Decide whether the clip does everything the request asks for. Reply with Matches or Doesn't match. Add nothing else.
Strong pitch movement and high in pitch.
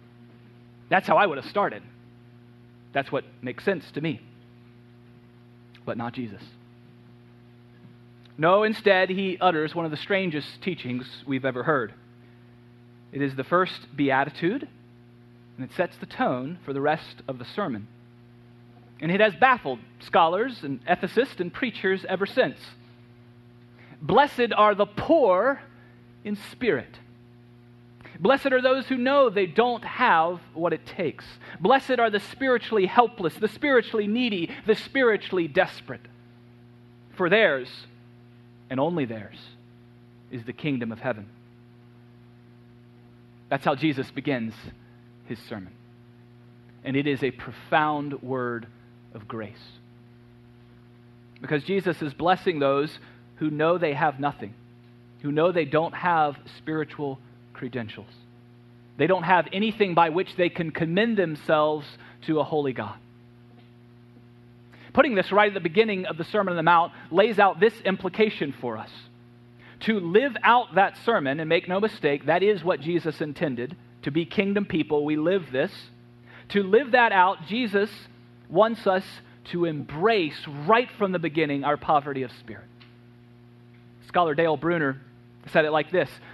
Doesn't match